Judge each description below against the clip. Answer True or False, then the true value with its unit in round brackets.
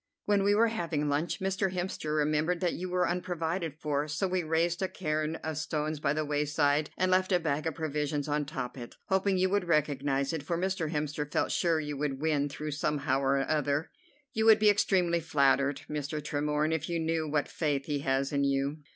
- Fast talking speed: True (210 wpm)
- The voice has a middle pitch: True (155 Hz)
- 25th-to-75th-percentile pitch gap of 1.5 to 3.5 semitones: True (3.1 semitones)